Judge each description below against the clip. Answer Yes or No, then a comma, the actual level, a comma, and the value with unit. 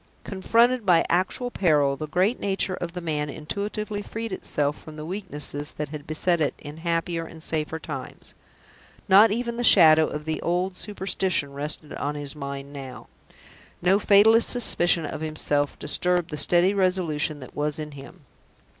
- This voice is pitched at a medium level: Yes, medium, 165 Hz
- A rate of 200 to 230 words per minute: No, average, 165 wpm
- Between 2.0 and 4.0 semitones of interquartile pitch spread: No, average, 4.4 semitones